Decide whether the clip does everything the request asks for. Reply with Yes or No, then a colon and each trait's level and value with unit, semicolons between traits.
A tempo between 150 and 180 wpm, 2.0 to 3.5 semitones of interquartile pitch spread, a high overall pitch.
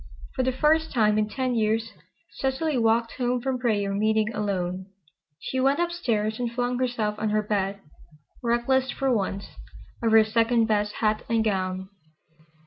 Yes: average, 160 wpm; average, 3.1 semitones; high, 225 Hz